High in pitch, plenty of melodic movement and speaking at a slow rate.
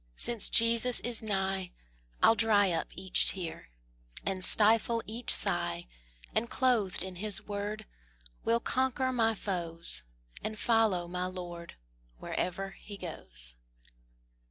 No: high, 200 Hz; average, 3.9 semitones; slow, 120 wpm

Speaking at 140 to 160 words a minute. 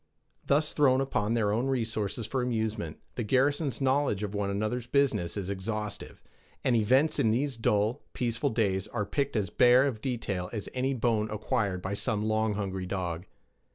No: average, 170 wpm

